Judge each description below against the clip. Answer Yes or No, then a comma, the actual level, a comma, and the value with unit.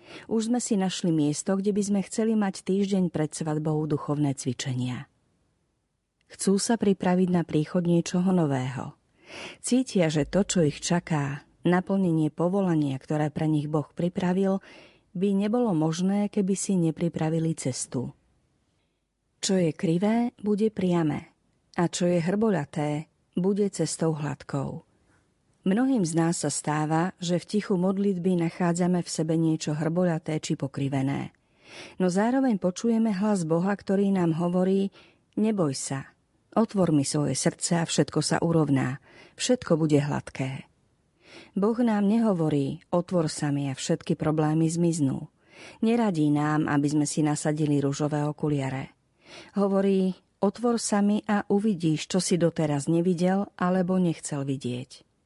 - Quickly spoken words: No, average, 130 wpm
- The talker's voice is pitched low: No, medium, 170 Hz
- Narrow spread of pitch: No, average, 4.4 semitones